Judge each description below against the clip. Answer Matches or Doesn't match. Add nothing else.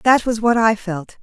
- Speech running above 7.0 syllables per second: Doesn't match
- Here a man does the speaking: Doesn't match